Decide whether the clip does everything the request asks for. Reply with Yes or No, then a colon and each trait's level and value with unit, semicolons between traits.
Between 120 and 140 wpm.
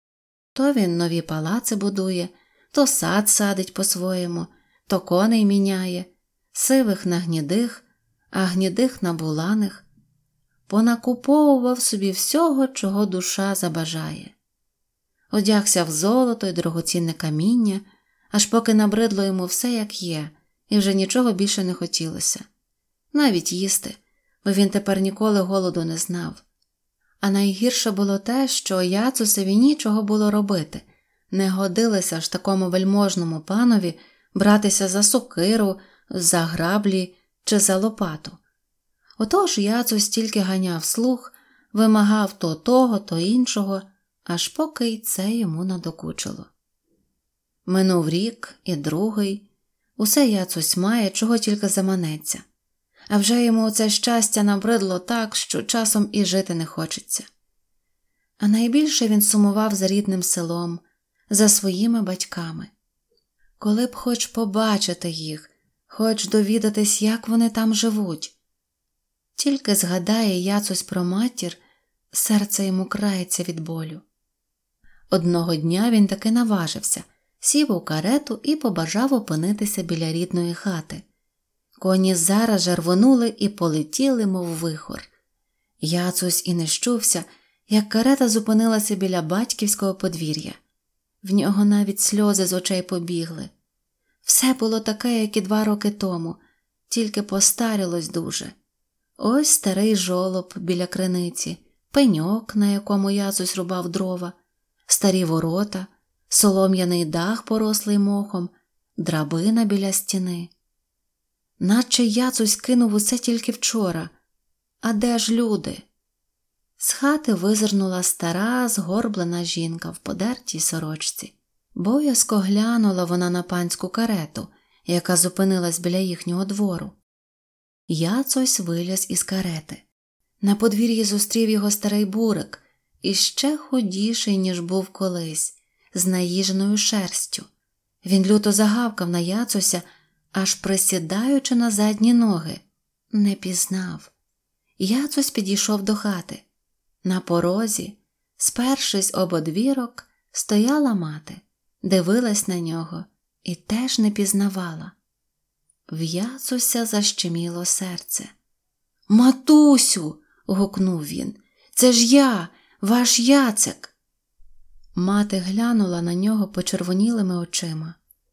No: average, 110 wpm